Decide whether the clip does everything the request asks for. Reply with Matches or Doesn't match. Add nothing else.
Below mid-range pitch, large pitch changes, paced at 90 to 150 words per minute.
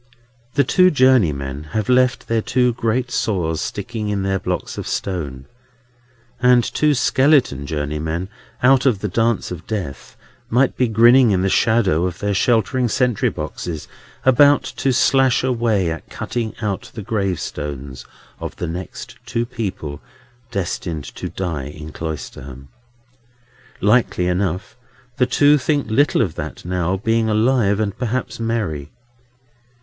Matches